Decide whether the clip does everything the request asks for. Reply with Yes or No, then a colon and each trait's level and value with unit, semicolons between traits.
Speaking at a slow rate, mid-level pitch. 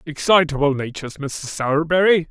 Yes: slow, 105 wpm; medium, 155 Hz